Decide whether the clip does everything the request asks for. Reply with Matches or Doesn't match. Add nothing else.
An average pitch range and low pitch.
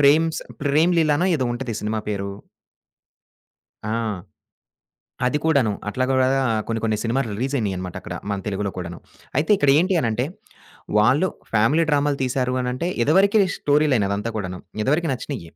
Doesn't match